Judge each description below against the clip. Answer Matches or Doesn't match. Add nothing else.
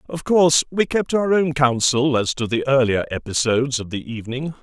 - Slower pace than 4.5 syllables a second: Doesn't match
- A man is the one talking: Matches